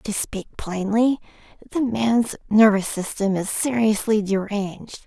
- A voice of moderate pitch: No, high, 215 Hz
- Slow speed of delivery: Yes, slow, 120 wpm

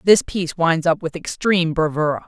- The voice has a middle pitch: Yes, medium, 170 Hz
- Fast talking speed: No, average, 185 wpm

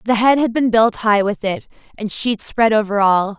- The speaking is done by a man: No, female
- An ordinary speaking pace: No, fast, 230 wpm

